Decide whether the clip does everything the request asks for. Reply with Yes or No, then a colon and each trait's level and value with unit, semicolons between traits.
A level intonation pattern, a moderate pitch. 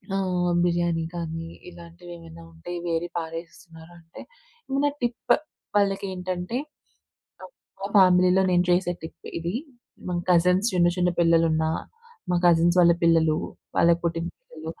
Yes: narrow, 1.5 semitones; medium, 175 Hz